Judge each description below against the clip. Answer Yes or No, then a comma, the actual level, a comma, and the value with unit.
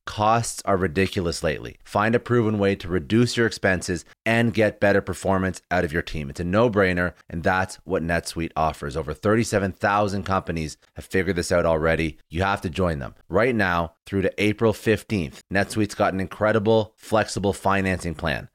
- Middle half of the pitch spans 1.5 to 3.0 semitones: No, average, 3.7 semitones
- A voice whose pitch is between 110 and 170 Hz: No, very low, 95 Hz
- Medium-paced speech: Yes, average, 180 wpm